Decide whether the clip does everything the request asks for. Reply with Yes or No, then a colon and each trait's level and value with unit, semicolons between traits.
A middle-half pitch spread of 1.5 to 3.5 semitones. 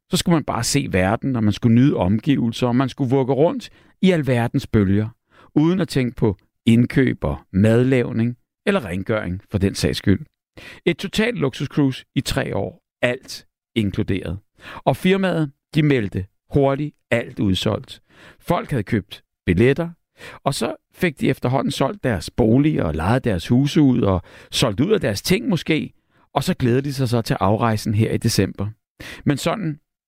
No: average, 5.2 semitones